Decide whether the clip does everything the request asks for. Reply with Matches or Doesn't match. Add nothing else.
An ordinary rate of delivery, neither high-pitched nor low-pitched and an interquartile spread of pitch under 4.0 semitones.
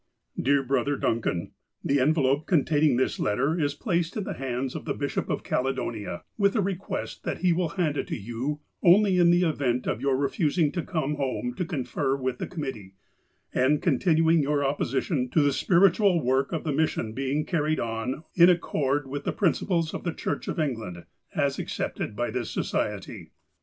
Doesn't match